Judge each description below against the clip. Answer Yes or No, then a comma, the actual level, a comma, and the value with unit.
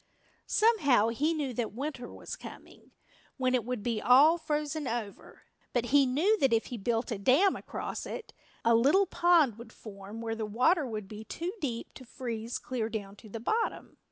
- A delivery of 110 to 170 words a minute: No, average, 185 wpm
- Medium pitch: No, very high, 250 Hz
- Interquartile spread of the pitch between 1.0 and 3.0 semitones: No, average, 4.9 semitones